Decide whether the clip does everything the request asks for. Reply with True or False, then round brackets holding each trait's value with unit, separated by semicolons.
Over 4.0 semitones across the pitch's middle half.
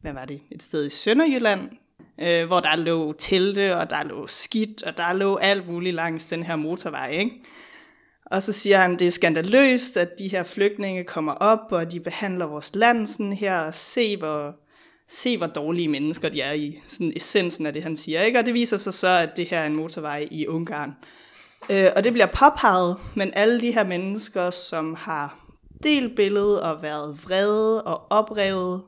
True (4.8 semitones)